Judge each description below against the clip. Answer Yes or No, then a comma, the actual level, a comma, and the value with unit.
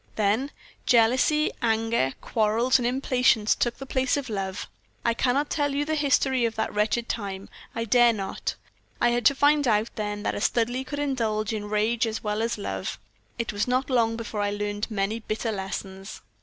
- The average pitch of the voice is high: Yes, high, 230 Hz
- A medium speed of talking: Yes, average, 185 wpm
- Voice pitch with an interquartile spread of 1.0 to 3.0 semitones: No, average, 3.4 semitones